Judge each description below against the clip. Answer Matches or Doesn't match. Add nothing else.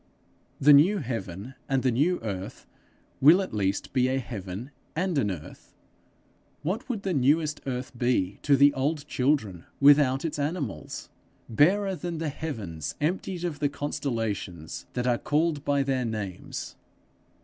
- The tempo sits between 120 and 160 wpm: Matches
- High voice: Doesn't match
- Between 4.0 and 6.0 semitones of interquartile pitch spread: Matches